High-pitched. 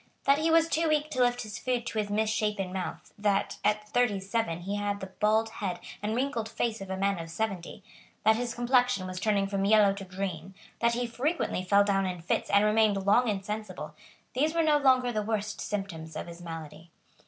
Yes: high, 210 Hz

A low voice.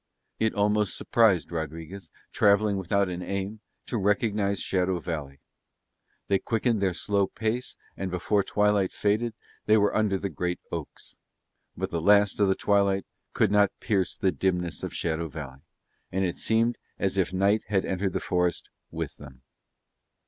Yes: low, 100 Hz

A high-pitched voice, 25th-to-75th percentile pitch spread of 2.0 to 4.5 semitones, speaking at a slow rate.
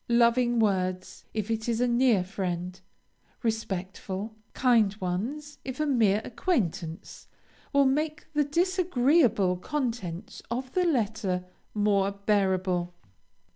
No: high, 220 Hz; wide, 5.4 semitones; slow, 110 wpm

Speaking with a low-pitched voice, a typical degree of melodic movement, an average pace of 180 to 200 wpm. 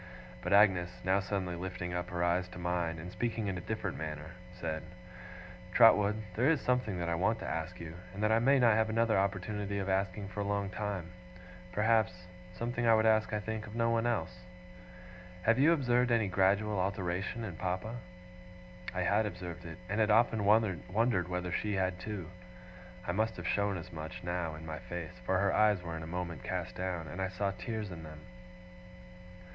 Yes: very low, 95 Hz; average, 3.6 semitones; average, 195 wpm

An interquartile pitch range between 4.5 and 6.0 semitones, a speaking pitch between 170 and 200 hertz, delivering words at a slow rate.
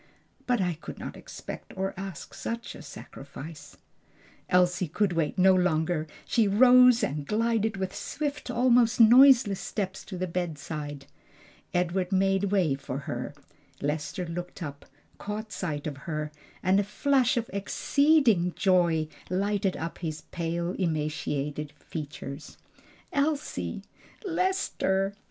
Yes: wide, 5.5 semitones; medium, 185 Hz; slow, 125 wpm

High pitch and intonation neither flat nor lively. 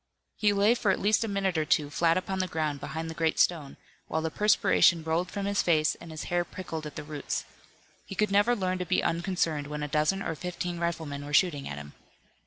No: medium, 170 Hz; average, 3.7 semitones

